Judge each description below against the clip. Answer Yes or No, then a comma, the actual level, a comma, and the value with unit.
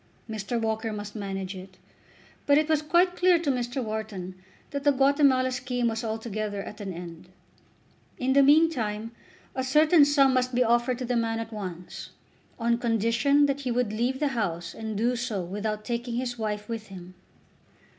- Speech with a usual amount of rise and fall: Yes, average, 3.9 semitones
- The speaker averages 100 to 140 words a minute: No, average, 175 wpm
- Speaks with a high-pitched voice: Yes, high, 235 Hz